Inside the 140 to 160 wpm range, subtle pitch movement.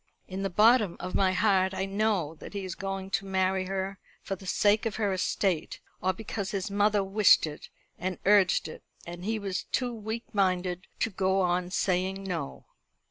No: average, 190 wpm; narrow, 1.7 semitones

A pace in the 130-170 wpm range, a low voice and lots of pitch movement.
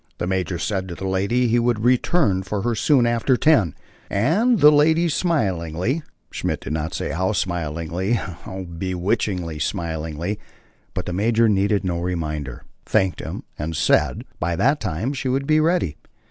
Yes: average, 160 wpm; very low, 95 Hz; wide, 6.1 semitones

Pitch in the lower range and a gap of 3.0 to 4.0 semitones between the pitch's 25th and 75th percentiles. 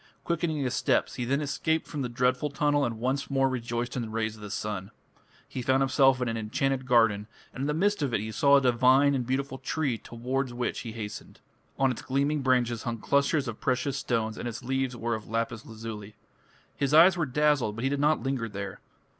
Yes: low, 130 Hz; average, 3.4 semitones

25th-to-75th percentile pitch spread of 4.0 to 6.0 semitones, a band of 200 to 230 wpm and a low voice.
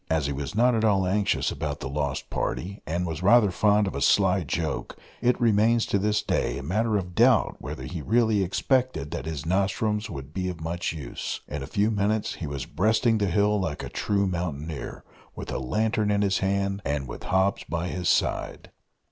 Yes: average, 4.7 semitones; fast, 205 wpm; very low, 95 Hz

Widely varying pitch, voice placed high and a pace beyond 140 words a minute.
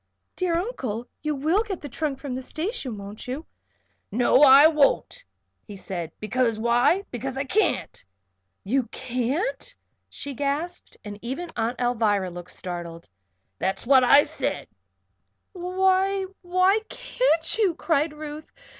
No: wide, 7.0 semitones; very high, 275 Hz; slow, 135 wpm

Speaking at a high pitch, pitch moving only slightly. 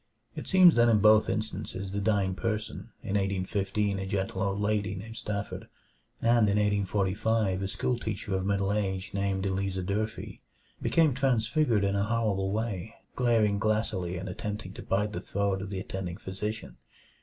No: low, 100 Hz; narrow, 2.2 semitones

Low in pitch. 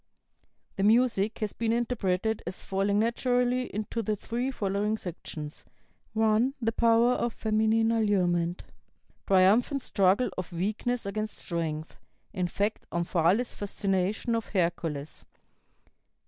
No: high, 210 Hz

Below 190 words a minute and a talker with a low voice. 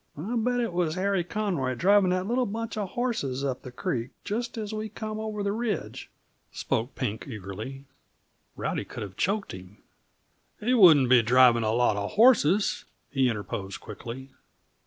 No: average, 165 wpm; medium, 170 Hz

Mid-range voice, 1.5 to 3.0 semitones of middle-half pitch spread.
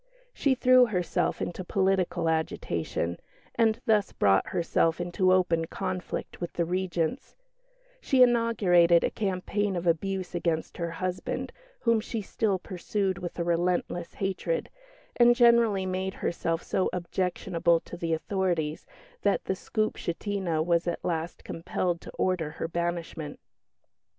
Yes: medium, 180 Hz; average, 2.7 semitones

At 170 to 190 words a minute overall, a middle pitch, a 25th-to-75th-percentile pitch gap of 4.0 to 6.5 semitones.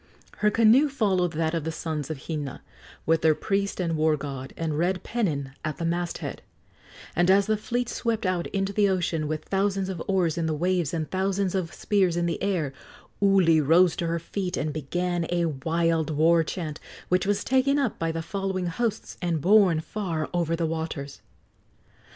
No: average, 185 wpm; medium, 170 Hz; average, 3.5 semitones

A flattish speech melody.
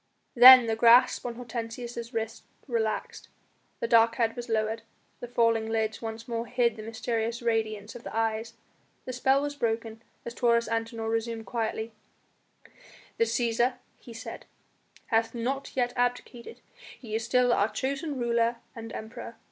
Yes: narrow, 1.4 semitones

